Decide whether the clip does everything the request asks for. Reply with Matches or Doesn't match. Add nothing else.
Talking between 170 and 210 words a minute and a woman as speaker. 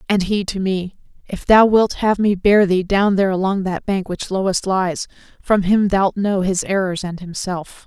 Matches